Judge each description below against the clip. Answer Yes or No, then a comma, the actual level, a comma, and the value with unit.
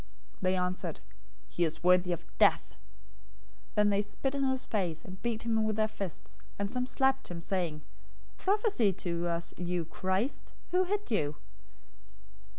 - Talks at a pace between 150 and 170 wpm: Yes, average, 160 wpm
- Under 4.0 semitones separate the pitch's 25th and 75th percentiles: No, average, 5.3 semitones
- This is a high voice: Yes, high, 195 Hz